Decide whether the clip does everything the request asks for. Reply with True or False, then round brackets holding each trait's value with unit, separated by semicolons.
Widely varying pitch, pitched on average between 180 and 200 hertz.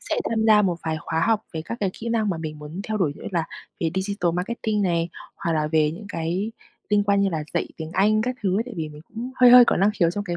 False (4.7 semitones; 190 Hz)